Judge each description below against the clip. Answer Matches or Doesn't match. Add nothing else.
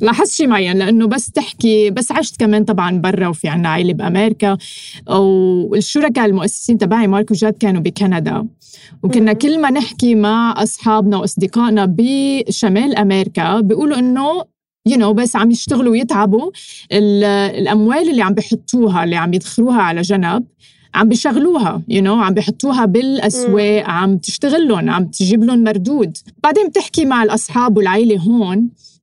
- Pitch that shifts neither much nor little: Matches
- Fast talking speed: Matches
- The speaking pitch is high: Matches